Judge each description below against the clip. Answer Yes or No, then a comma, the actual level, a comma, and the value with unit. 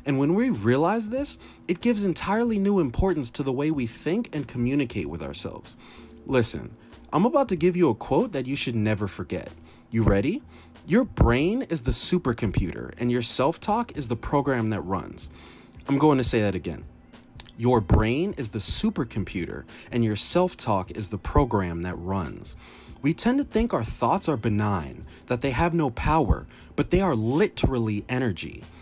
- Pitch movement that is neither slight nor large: No, wide, 6.5 semitones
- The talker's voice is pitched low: Yes, low, 120 Hz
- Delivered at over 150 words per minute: Yes, average, 180 wpm